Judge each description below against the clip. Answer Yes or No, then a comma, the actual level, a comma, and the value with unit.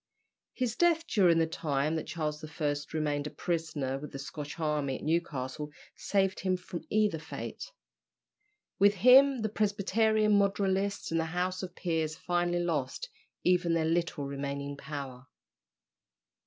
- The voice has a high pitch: No, medium, 165 Hz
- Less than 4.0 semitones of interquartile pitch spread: No, average, 4.7 semitones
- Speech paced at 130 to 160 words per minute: Yes, average, 140 wpm